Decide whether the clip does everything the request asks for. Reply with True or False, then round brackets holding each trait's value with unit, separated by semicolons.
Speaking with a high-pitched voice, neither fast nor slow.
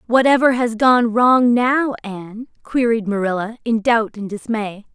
True (230 Hz; 145 wpm)